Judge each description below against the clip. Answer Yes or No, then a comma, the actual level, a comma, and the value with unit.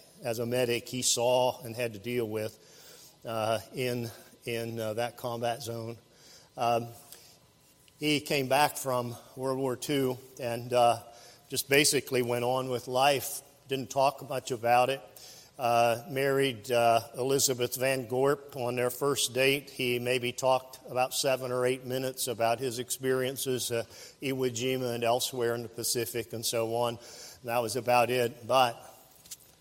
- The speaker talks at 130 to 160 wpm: Yes, average, 155 wpm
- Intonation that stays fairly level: Yes, narrow, 1.9 semitones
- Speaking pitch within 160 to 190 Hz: No, low, 125 Hz